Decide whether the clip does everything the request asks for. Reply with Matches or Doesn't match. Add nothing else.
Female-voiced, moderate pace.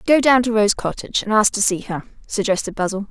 Doesn't match